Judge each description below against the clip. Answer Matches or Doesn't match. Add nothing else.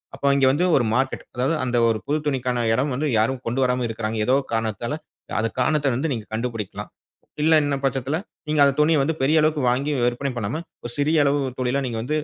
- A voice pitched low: Matches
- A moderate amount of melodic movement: Matches